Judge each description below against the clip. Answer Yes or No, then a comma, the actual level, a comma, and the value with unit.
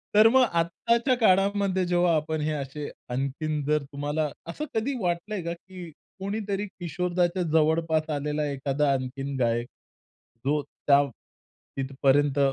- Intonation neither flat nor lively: Yes, average, 4.5 semitones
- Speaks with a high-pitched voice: No, medium, 155 Hz